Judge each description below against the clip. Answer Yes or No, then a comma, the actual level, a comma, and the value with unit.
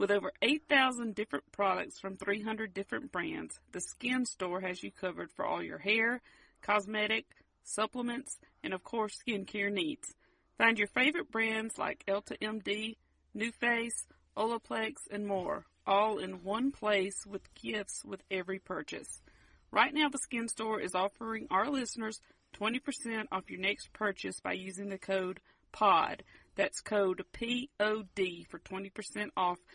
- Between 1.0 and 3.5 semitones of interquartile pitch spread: Yes, average, 2.9 semitones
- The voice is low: No, high, 210 Hz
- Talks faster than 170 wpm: No, average, 145 wpm